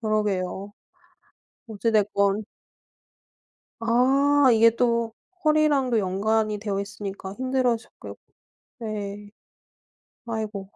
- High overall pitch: Yes, high, 220 Hz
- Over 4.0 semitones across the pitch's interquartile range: No, average, 2.8 semitones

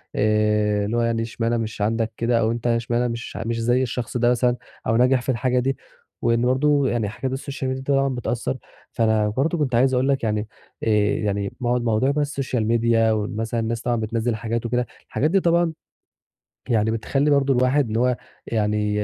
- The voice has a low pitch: Yes, low, 120 Hz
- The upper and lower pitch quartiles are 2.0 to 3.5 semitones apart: Yes, average, 2.7 semitones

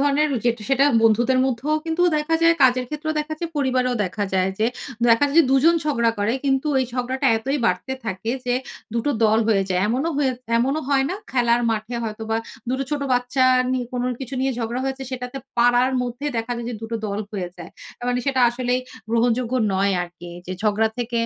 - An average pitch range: Yes, average, 3.1 semitones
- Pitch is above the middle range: Yes, high, 245 Hz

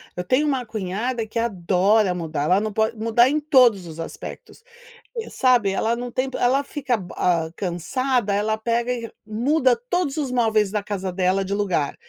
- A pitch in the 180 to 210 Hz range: No, high, 220 Hz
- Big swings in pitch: No, average, 4.7 semitones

